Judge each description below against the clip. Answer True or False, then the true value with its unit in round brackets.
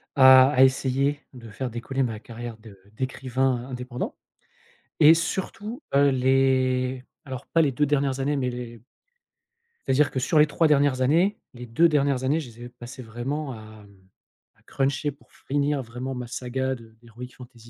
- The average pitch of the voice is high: False (130 Hz)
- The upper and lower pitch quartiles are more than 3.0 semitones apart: False (2.7 semitones)